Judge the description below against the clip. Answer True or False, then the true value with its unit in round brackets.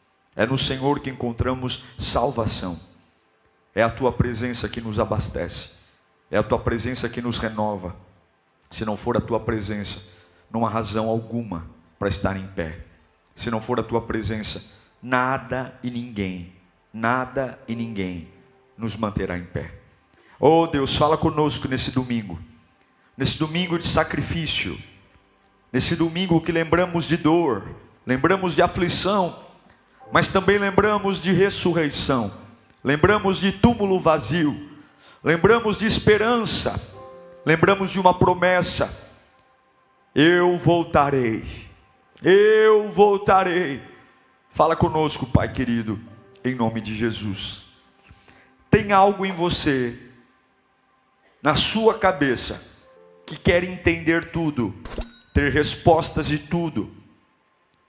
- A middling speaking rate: False (115 wpm)